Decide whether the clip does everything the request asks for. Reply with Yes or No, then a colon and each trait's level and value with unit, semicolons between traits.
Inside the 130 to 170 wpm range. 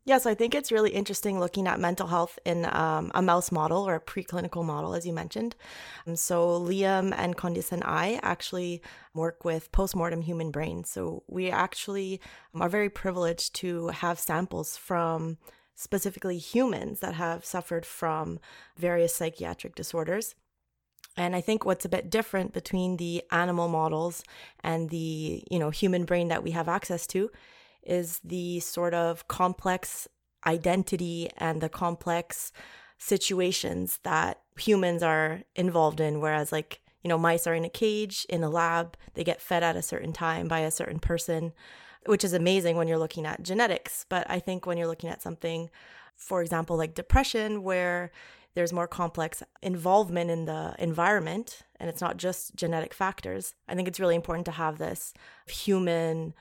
Yes: average, 165 wpm